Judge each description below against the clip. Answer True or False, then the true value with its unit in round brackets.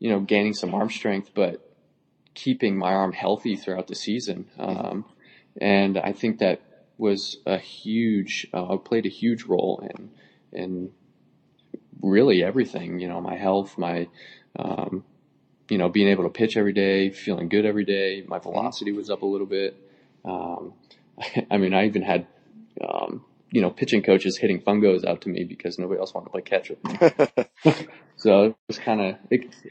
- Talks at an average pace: True (175 wpm)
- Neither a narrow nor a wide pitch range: False (1.7 semitones)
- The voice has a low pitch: True (100 Hz)